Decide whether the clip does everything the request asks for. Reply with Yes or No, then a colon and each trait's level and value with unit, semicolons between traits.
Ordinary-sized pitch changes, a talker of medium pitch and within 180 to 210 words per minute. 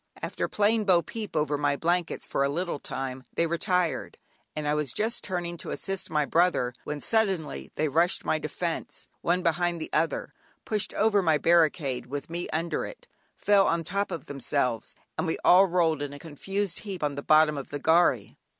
Yes: average, 3.7 semitones; medium, 165 Hz; average, 185 wpm